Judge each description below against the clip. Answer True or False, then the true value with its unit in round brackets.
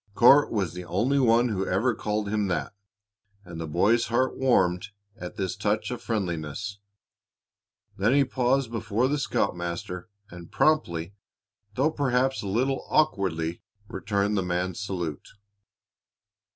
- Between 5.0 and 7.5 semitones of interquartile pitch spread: True (5.6 semitones)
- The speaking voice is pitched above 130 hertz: False (105 Hz)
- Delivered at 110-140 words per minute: True (135 wpm)